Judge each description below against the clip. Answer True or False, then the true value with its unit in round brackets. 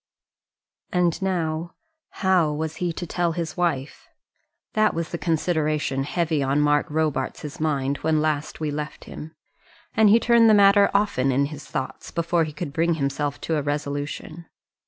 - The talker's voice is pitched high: False (160 Hz)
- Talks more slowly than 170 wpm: True (160 wpm)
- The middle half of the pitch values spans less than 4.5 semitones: True (2.9 semitones)